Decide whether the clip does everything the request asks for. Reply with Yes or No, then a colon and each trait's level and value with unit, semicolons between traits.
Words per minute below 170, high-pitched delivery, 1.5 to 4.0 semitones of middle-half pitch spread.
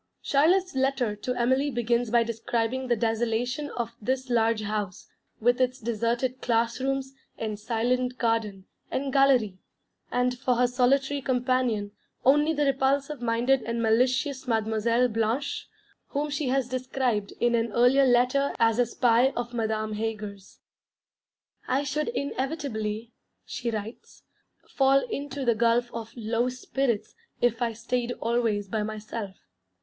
Yes: slow, 135 wpm; high, 240 Hz; average, 2.7 semitones